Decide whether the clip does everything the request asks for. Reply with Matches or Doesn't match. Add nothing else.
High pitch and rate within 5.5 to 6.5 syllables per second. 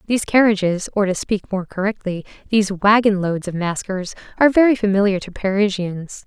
Matches